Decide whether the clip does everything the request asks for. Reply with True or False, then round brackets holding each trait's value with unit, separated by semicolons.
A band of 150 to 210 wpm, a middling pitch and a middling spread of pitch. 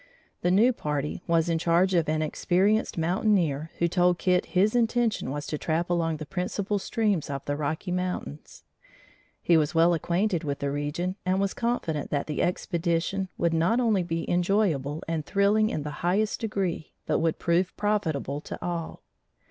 True (170 wpm; 175 Hz; 3.7 semitones)